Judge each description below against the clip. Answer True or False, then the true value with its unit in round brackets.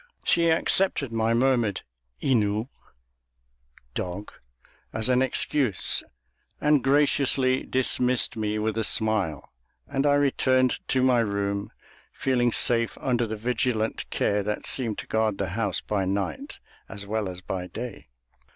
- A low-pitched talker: True (115 Hz)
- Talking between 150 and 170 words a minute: False (135 wpm)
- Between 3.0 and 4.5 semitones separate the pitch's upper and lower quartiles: True (3.9 semitones)